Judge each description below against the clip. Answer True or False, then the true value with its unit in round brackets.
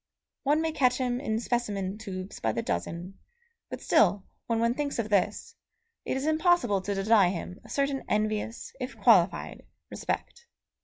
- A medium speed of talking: True (160 wpm)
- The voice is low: False (220 Hz)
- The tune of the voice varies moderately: False (5.7 semitones)